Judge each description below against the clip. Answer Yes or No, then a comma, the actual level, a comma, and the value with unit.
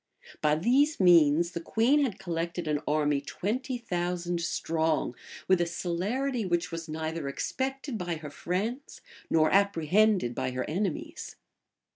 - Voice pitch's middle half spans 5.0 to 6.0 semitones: Yes, wide, 5.6 semitones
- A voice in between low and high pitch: Yes, medium, 175 Hz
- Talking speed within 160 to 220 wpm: No, slow, 135 wpm